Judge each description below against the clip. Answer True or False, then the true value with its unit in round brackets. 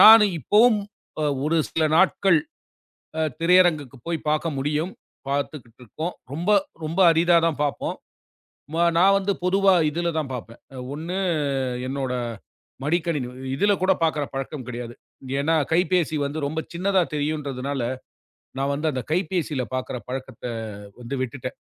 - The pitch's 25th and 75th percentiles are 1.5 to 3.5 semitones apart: False (4.3 semitones)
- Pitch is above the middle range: False (155 Hz)